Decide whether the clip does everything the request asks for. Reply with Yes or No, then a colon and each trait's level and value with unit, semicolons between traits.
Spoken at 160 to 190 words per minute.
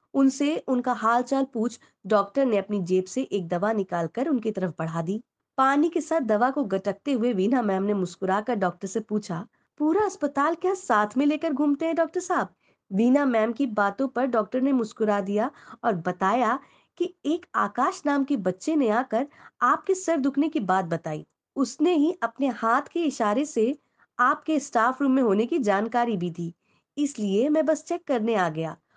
Yes: average, 185 wpm